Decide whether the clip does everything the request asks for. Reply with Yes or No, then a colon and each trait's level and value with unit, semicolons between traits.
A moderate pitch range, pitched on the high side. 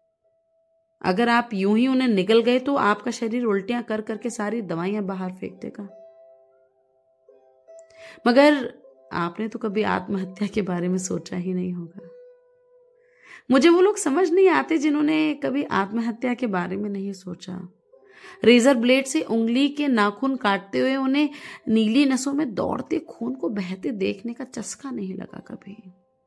No: wide, 6.6 semitones; high, 235 Hz